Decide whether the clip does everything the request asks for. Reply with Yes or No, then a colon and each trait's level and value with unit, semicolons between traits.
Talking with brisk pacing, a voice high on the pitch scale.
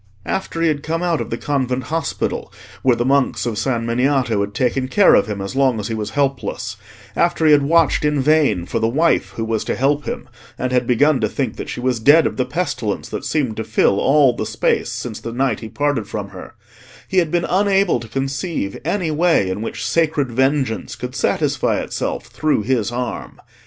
No: fast, 215 wpm; low, 130 Hz